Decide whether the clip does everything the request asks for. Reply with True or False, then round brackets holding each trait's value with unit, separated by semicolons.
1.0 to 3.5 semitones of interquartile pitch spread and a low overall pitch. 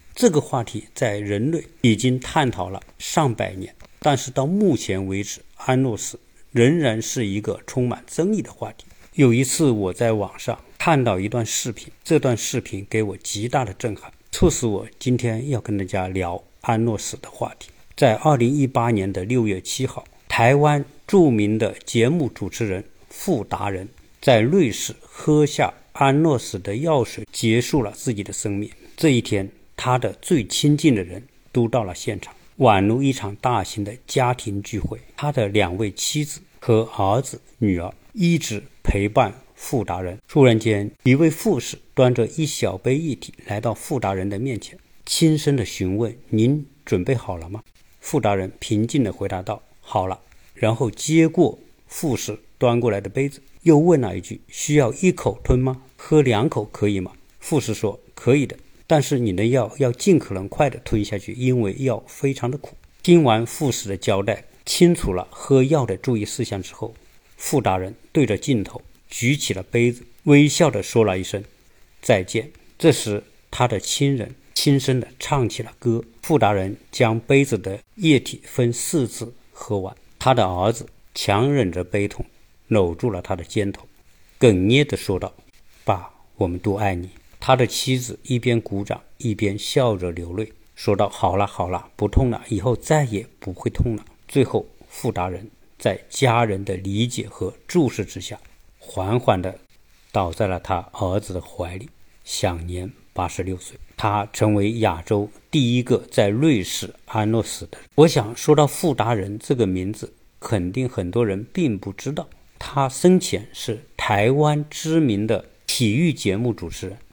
False (5.1 semitones; 115 Hz)